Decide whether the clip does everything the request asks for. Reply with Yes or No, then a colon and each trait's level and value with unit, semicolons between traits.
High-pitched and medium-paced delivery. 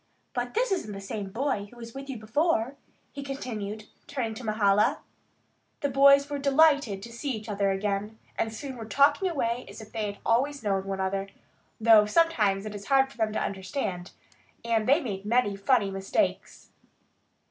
Yes: high, 225 Hz; average, 180 wpm